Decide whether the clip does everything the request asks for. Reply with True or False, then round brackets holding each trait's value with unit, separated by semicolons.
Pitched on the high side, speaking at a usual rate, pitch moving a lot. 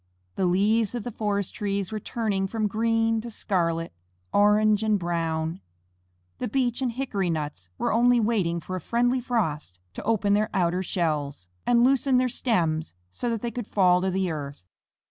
False (205 Hz; 175 wpm; 5.0 semitones)